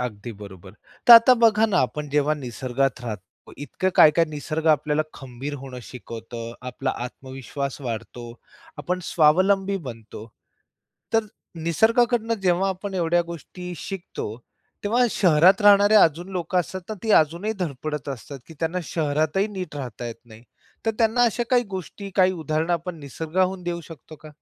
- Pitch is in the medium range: Yes, medium, 160 Hz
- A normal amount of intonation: No, wide, 5.8 semitones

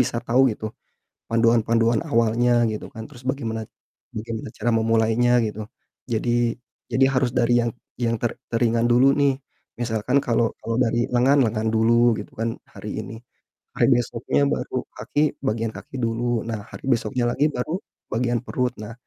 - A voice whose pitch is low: Yes, low, 115 Hz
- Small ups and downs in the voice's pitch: Yes, narrow, 1.4 semitones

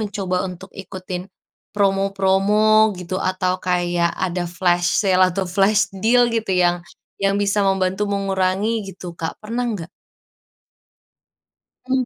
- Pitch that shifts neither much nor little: No, narrow, 1.6 semitones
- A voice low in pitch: No, high, 190 Hz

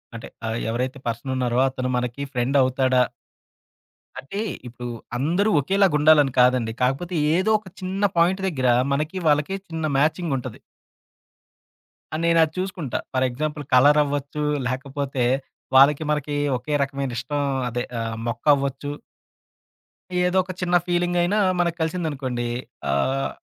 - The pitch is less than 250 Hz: Yes, medium, 140 Hz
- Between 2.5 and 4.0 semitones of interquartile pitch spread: No, average, 4.6 semitones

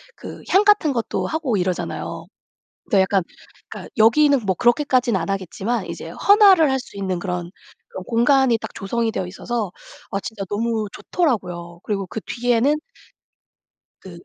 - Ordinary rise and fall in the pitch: No, wide, 5.8 semitones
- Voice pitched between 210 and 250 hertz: Yes, high, 225 Hz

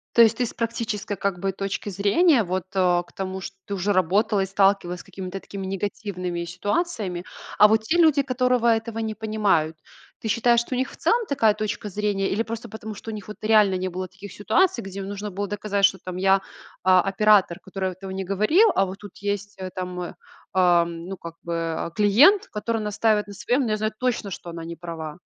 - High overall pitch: Yes, high, 200 Hz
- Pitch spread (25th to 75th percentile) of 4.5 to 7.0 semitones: No, average, 2.8 semitones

